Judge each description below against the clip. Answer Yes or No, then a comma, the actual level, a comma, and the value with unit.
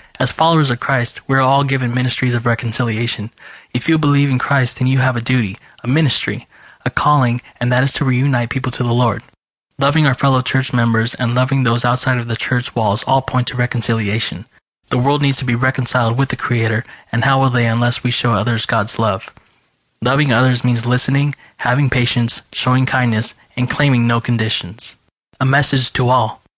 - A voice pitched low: Yes, low, 125 Hz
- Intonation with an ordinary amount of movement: No, narrow, 2.1 semitones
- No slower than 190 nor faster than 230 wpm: Yes, average, 195 wpm